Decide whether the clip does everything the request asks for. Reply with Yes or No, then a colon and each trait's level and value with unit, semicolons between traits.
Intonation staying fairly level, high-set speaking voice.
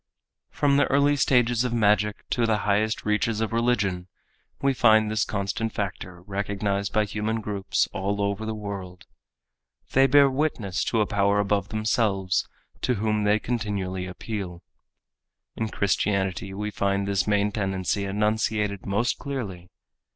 No: narrow, 2.1 semitones; low, 105 Hz